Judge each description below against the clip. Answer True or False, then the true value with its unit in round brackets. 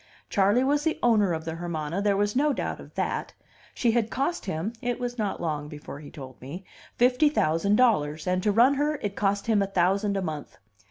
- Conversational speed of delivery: False (210 wpm)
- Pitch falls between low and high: False (200 Hz)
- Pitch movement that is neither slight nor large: False (6.6 semitones)